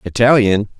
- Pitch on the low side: Yes, low, 110 Hz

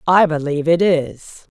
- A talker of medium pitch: Yes, medium, 160 Hz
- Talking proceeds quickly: No, average, 155 wpm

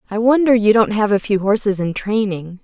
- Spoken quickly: Yes, fast, 230 wpm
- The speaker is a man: No, female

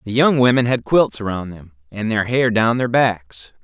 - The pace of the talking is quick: Yes, fast, 215 wpm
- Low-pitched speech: Yes, low, 115 Hz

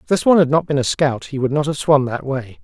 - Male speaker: Yes, male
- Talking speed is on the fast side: Yes, fast, 340 wpm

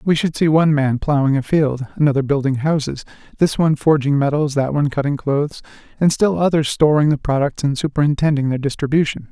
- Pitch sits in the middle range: Yes, medium, 145 Hz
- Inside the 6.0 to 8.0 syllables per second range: Yes, 6.1 syllables/s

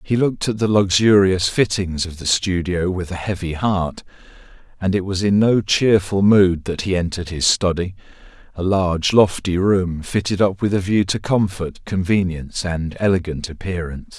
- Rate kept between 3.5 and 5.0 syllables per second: Yes, 4.9 syllables/s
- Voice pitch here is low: Yes, very low, 95 Hz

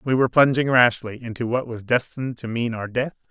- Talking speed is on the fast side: Yes, fast, 220 wpm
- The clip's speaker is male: Yes, male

